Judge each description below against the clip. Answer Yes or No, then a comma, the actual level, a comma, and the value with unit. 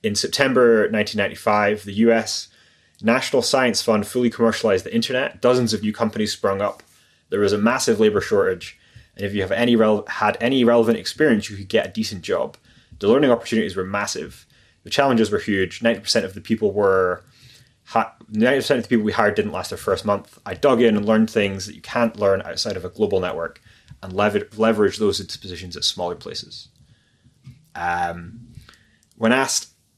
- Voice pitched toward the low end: Yes, low, 110 Hz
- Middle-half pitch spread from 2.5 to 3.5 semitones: Yes, average, 2.9 semitones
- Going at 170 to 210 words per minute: Yes, average, 180 wpm